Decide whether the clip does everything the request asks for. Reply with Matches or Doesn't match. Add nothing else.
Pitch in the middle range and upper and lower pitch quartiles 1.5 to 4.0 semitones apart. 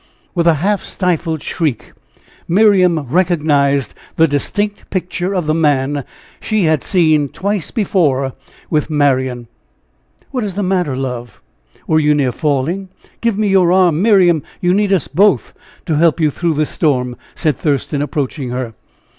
Doesn't match